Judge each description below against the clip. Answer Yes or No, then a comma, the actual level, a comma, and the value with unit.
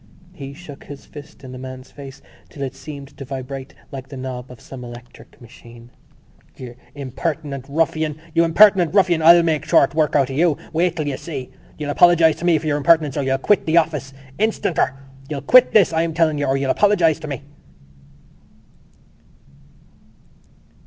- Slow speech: No, average, 175 wpm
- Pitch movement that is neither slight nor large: Yes, average, 3.5 semitones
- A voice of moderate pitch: Yes, medium, 145 Hz